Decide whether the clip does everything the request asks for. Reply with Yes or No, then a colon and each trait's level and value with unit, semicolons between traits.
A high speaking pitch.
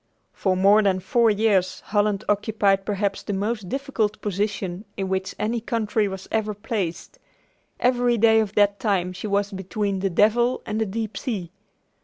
Yes: high, 205 Hz